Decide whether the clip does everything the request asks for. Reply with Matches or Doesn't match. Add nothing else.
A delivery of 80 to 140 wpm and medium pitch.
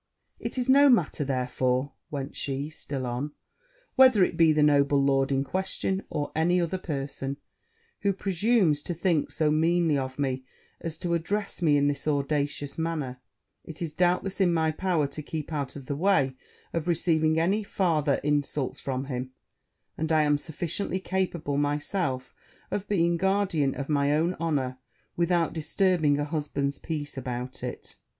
Doesn't match